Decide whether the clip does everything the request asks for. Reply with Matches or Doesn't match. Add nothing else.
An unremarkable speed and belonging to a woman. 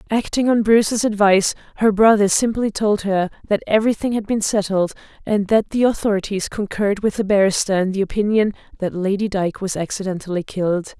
Matches